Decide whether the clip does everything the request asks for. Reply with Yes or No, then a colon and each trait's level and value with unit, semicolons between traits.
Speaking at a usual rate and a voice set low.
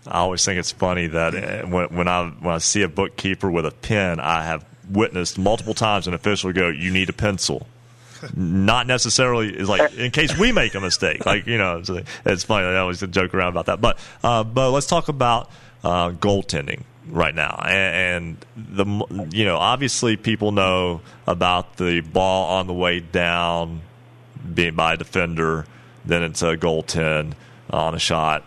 Yes: average, 185 wpm; very low, 95 Hz